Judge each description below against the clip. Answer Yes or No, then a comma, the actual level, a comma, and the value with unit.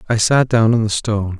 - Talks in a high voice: No, low, 110 Hz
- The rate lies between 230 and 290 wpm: Yes, fast, 260 wpm